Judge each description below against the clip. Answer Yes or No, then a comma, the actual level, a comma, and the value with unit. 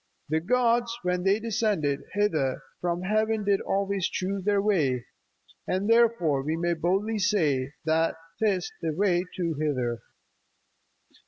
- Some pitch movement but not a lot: Yes, average, 4.7 semitones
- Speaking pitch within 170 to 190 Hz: Yes, medium, 185 Hz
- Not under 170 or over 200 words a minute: No, slow, 135 wpm